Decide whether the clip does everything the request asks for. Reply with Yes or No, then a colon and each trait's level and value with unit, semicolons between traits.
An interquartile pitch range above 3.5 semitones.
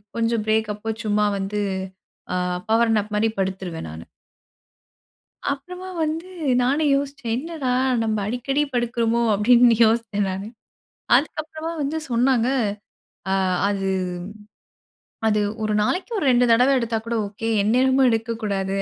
Yes: average, 4.2 semitones